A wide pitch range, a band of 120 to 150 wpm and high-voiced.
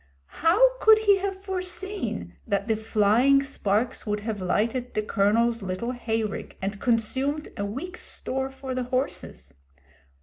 Yes: wide, 6.3 semitones; average, 145 wpm; high, 245 Hz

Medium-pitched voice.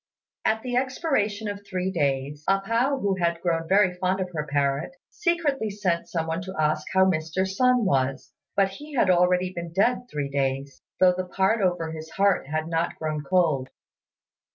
Yes: medium, 180 Hz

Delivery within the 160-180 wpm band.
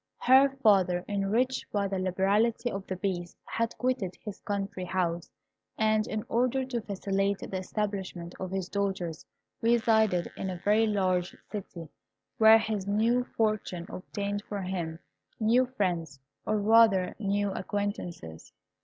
No: slow, 135 wpm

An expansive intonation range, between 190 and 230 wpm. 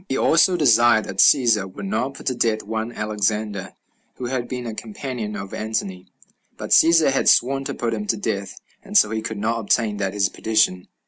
No: average, 3.3 semitones; average, 200 wpm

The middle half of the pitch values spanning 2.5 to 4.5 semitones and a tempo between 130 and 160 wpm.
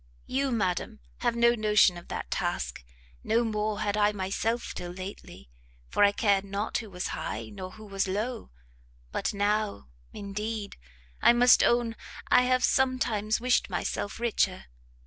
Yes: average, 2.9 semitones; average, 155 wpm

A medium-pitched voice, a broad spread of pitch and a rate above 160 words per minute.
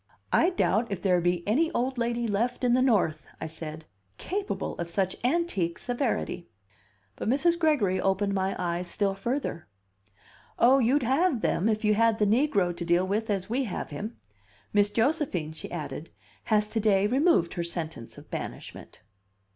No: high, 210 Hz; wide, 5.9 semitones; average, 170 wpm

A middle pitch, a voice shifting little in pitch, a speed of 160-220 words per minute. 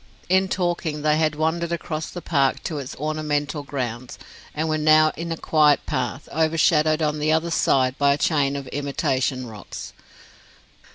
Yes: medium, 150 Hz; narrow, 2.2 semitones; average, 165 wpm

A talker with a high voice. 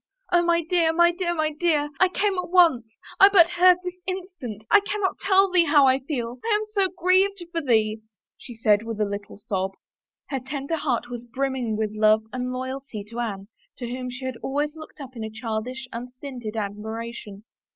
Yes: very high, 265 Hz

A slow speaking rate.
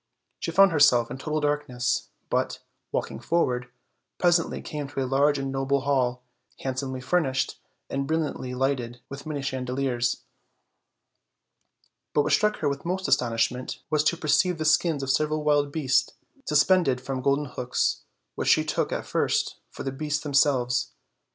No: average, 155 wpm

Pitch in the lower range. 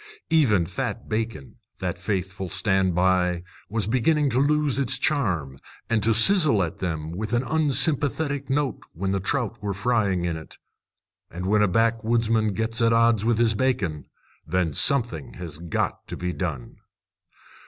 Yes: low, 110 Hz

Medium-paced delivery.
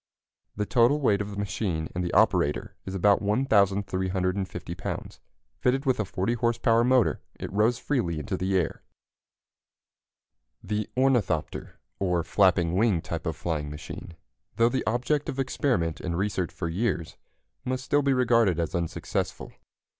Yes: average, 145 wpm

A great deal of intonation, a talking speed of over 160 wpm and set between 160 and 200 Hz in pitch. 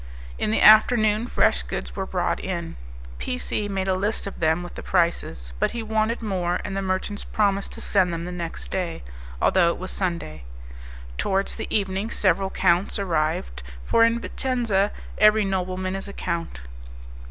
No: average, 3.5 semitones; average, 175 wpm; high, 190 Hz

